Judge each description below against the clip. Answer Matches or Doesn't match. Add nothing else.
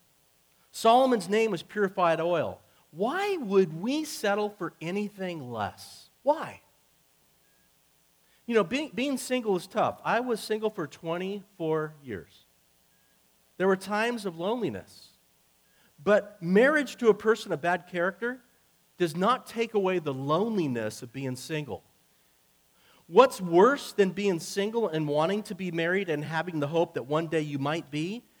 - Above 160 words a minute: Doesn't match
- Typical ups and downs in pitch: Doesn't match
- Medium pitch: Matches